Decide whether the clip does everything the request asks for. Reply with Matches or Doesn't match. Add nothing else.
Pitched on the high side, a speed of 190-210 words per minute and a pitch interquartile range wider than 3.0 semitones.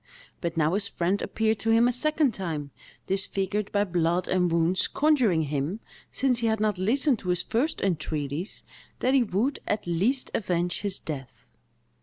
Doesn't match